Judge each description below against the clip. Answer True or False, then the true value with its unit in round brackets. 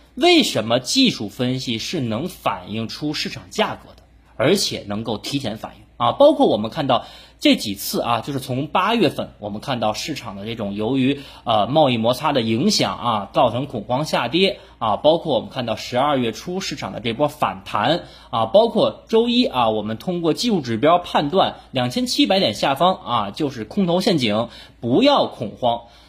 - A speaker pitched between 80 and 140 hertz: True (135 Hz)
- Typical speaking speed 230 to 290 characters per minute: True (275 characters per minute)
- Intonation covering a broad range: True (8.9 semitones)